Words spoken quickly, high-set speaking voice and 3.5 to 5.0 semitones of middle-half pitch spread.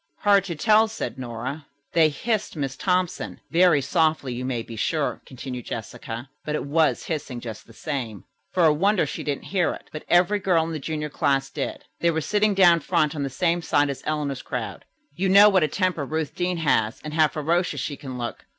No: fast, 210 wpm; medium, 155 Hz; average, 4.5 semitones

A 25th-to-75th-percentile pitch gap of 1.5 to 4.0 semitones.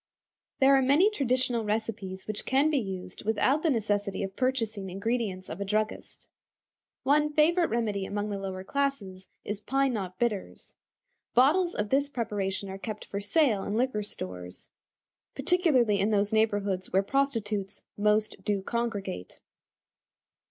No: average, 4.9 semitones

